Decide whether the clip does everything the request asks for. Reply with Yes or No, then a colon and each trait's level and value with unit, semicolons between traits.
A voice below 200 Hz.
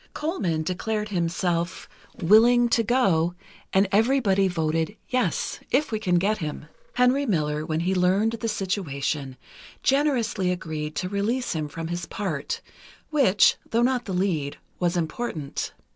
Yes: high, 190 Hz